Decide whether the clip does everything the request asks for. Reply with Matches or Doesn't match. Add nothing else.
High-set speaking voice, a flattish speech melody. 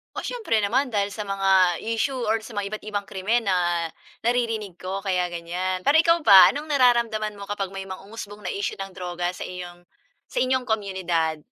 Doesn't match